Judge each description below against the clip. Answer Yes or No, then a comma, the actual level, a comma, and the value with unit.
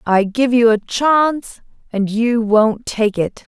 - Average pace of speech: Yes, average, 170 wpm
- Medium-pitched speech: No, high, 230 Hz